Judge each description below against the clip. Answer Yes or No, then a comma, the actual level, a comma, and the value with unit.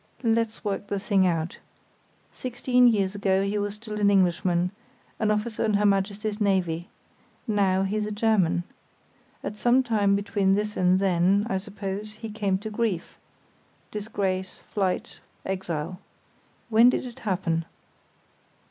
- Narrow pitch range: Yes, narrow, 2.1 semitones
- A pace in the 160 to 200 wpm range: No, slow, 135 wpm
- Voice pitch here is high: Yes, high, 200 Hz